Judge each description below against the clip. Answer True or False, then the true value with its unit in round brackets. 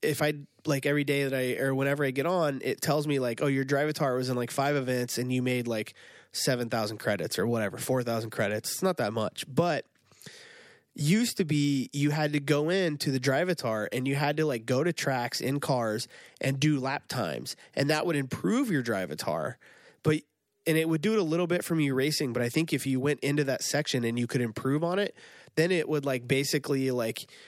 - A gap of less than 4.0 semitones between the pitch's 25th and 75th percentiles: True (3.0 semitones)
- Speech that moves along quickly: True (225 wpm)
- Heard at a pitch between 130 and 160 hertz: True (140 Hz)